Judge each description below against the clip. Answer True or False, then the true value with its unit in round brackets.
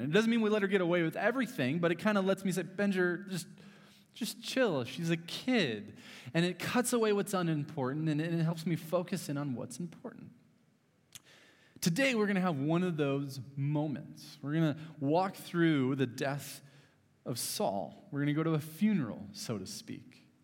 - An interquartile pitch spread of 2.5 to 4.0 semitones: False (5.2 semitones)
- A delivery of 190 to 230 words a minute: True (195 wpm)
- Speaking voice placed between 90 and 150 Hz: False (170 Hz)